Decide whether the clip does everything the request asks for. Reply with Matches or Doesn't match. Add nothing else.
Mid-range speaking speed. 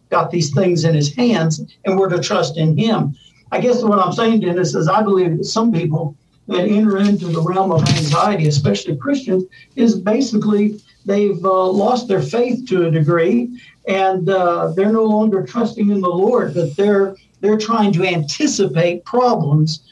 Matches